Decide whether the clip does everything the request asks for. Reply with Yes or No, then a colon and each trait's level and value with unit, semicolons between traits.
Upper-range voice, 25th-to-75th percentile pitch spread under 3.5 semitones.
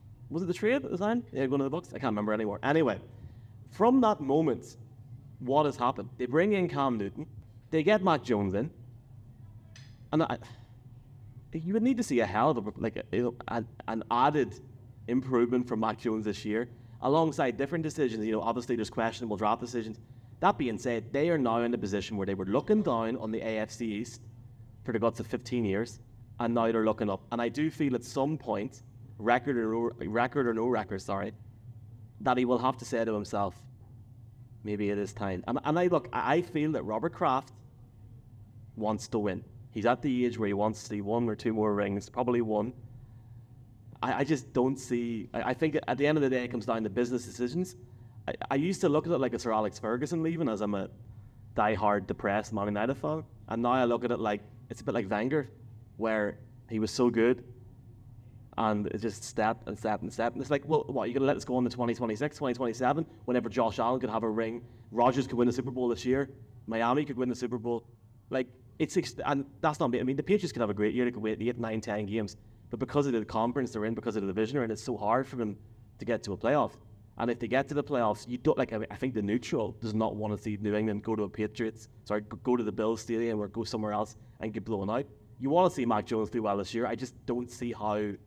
No: low, 120 Hz; narrow, 2.5 semitones